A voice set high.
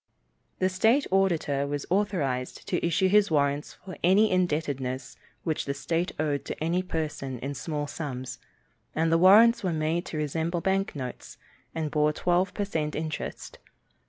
No: medium, 160 Hz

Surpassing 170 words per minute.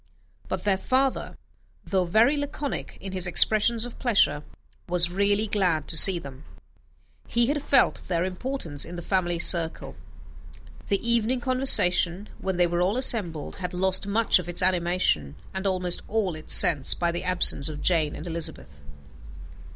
No: average, 160 wpm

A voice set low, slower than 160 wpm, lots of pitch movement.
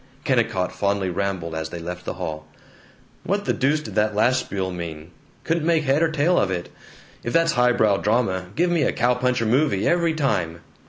No: low, 110 Hz; average, 195 wpm; wide, 8.6 semitones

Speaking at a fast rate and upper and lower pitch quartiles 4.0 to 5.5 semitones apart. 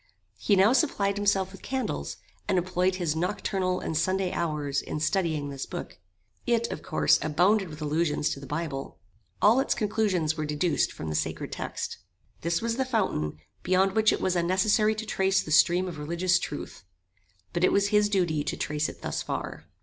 No: average, 185 wpm; average, 4.7 semitones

